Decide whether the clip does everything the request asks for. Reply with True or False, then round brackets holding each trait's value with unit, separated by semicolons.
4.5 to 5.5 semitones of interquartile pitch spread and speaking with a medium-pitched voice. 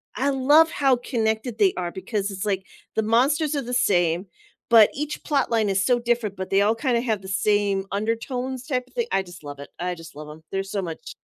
False (4.8 semitones; 215 Hz)